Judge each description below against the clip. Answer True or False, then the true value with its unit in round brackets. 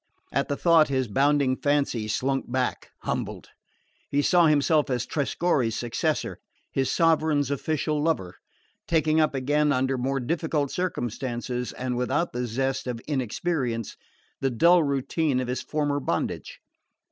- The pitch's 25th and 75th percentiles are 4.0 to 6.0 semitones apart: False (3.3 semitones)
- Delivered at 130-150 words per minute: True (135 wpm)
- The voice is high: False (140 Hz)